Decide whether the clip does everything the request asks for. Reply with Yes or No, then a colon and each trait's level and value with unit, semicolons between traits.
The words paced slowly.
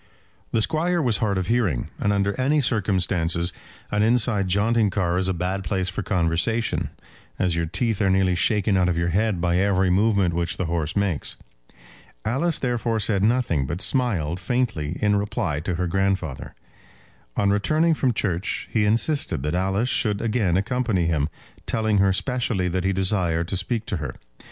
No: average, 175 wpm